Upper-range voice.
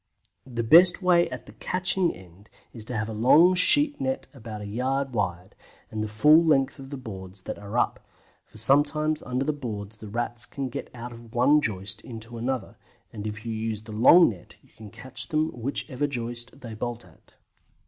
No: low, 120 Hz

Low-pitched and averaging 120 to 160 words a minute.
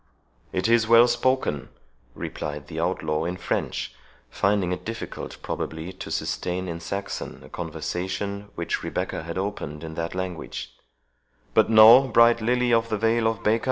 Yes: low, 100 Hz; average, 155 wpm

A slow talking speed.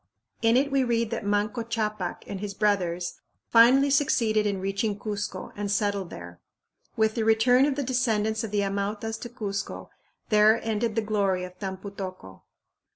No: average, 165 wpm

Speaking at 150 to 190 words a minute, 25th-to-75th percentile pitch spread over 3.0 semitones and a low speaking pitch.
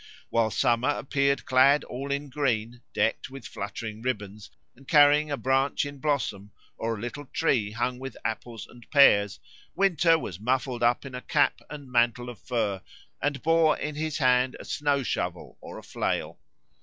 Yes: average, 170 wpm; average, 3.7 semitones; low, 130 Hz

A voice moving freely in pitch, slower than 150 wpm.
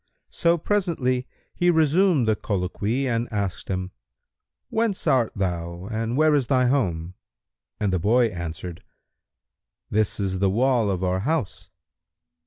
Yes: wide, 6.7 semitones; slow, 135 wpm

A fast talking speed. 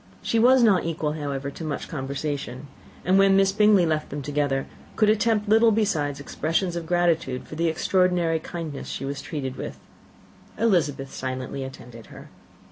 No: average, 160 wpm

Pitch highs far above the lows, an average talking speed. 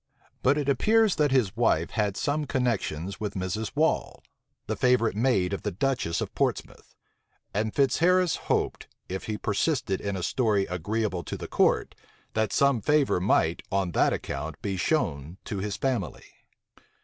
Yes: wide, 6.1 semitones; average, 160 wpm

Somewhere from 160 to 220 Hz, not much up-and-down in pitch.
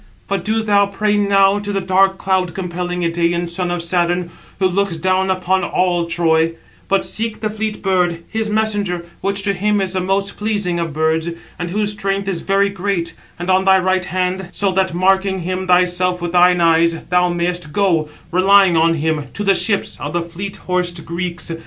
Yes: medium, 185 Hz; narrow, 2.3 semitones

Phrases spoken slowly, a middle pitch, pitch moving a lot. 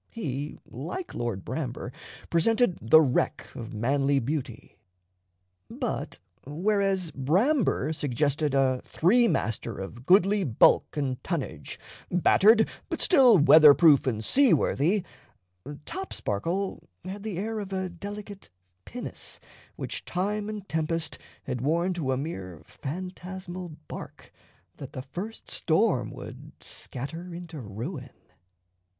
Yes: slow, 115 wpm; medium, 165 Hz; wide, 6.7 semitones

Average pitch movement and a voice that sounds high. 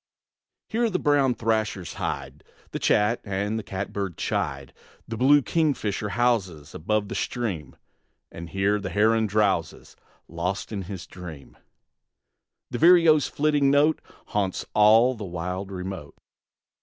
No: average, 4.9 semitones; low, 105 Hz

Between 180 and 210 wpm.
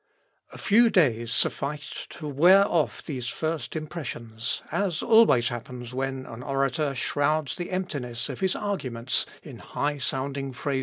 No: average, 145 wpm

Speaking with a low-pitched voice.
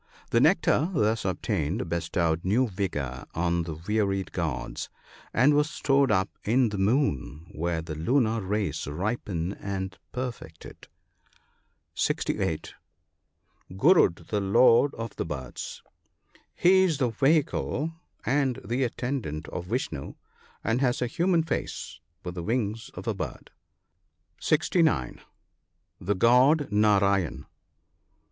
Yes: low, 105 Hz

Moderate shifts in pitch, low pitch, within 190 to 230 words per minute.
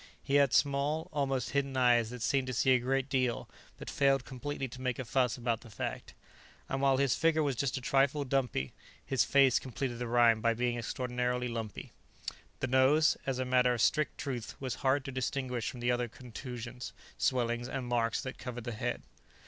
No: narrow, 2.0 semitones; low, 130 Hz; average, 195 wpm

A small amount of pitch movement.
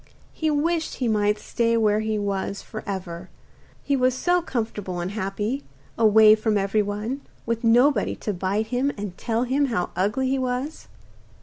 No: average, 3.9 semitones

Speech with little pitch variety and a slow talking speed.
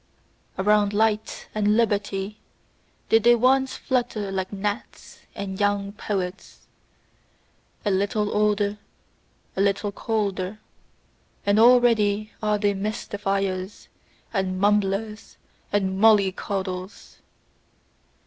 Yes: narrow, 1.6 semitones; slow, 90 wpm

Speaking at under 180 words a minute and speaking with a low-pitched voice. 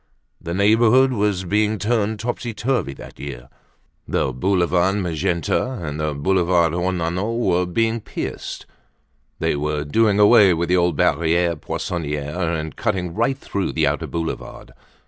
Yes: average, 140 wpm; very low, 90 Hz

